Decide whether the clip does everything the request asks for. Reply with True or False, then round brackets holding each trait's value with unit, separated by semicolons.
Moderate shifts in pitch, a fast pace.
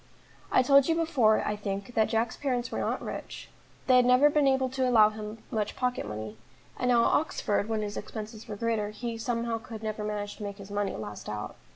True (3.2 semitones; 220 wpm)